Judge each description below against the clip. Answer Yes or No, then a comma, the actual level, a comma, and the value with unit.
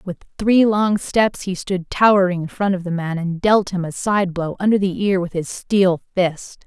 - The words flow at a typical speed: No, fast, 225 wpm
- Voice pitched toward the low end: No, medium, 185 Hz